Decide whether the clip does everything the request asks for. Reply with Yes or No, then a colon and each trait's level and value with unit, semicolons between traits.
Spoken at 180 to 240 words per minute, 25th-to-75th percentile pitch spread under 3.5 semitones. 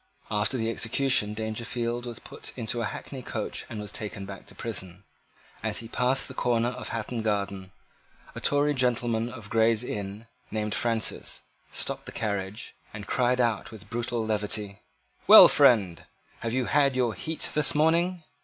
No: average, 165 wpm; average, 2.9 semitones